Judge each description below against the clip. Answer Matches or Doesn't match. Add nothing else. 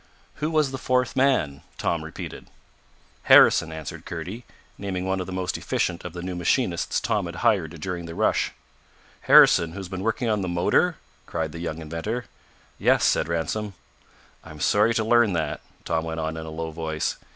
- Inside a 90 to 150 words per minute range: Doesn't match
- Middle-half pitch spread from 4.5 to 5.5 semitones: Matches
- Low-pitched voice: Matches